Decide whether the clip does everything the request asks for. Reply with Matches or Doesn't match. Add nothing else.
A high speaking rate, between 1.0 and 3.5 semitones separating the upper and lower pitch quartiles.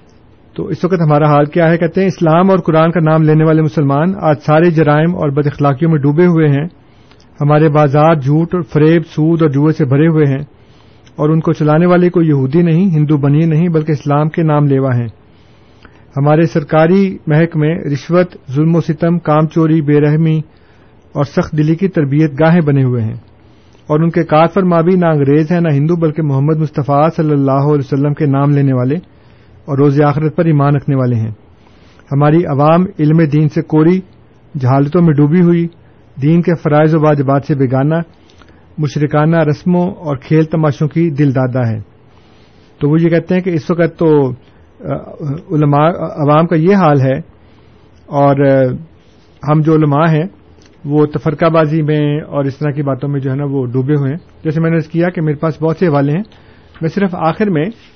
Matches